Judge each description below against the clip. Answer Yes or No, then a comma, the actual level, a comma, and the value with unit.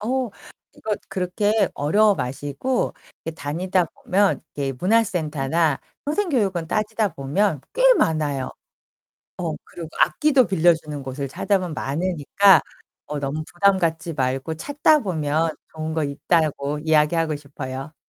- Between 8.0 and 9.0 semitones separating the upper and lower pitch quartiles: No, average, 5.3 semitones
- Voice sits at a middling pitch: Yes, medium, 165 Hz